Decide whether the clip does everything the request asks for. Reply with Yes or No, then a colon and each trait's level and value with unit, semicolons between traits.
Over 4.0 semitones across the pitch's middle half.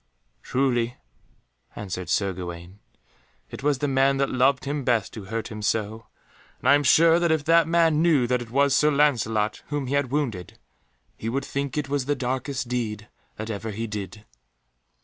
Yes: average, 4.6 semitones